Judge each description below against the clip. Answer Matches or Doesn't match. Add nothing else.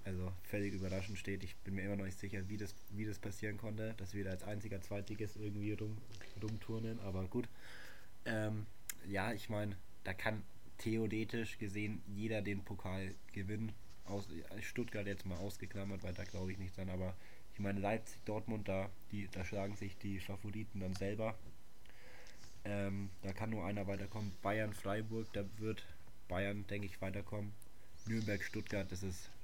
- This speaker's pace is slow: Doesn't match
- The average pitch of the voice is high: Doesn't match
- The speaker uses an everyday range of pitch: Doesn't match